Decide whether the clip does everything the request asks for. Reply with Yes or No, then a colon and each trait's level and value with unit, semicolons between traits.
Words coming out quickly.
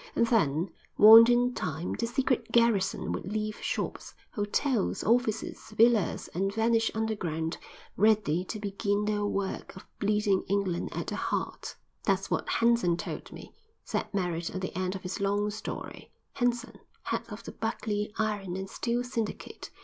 No: average, 155 wpm